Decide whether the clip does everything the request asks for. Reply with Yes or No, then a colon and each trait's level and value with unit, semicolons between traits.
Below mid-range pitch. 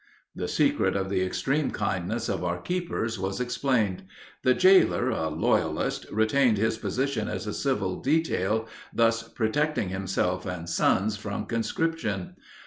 Yes: low, 110 Hz